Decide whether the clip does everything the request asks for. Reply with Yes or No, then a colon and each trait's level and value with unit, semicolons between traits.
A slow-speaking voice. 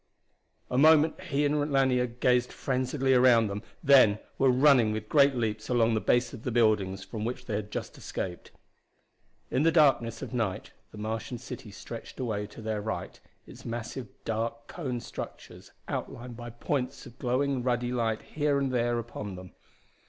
No: average, 170 wpm